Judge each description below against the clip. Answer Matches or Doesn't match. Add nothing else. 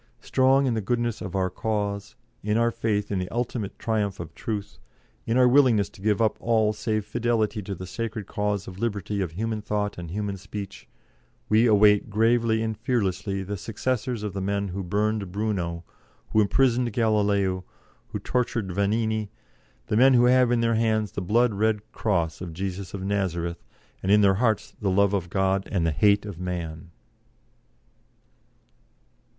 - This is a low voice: Matches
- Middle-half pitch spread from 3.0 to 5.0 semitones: Doesn't match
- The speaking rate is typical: Matches